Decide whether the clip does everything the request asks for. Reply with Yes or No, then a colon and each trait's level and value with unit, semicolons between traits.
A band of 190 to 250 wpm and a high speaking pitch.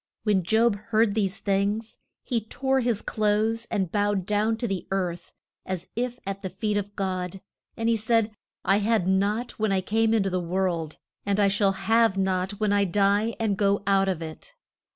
Yes: average, 195 wpm; high, 205 Hz